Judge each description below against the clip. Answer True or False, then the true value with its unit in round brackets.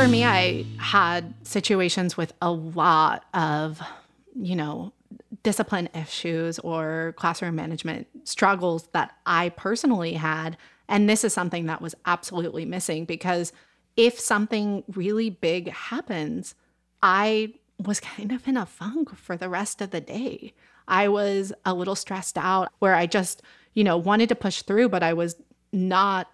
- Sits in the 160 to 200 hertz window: True (185 Hz)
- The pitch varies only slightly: False (3.8 semitones)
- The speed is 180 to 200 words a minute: False (155 wpm)